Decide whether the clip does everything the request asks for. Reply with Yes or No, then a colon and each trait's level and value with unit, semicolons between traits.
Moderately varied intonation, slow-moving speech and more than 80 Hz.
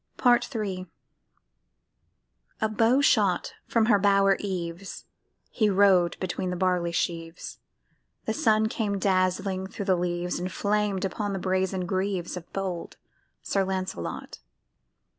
No: narrow, 2.2 semitones; slow, 125 wpm; high, 190 Hz